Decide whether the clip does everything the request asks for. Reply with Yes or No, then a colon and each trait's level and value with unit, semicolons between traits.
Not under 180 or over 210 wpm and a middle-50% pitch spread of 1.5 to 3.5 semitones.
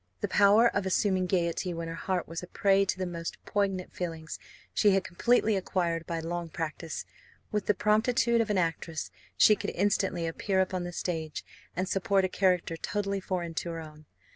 Yes: average, 190 wpm; average, 2.9 semitones